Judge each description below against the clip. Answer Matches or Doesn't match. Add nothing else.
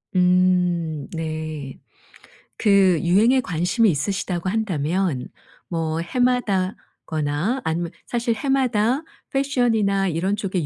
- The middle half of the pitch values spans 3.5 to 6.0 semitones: Matches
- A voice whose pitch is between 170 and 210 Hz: Matches